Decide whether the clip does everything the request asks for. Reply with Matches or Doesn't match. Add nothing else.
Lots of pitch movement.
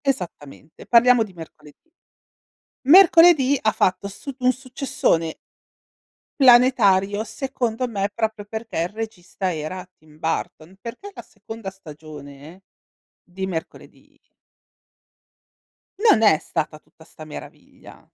Matches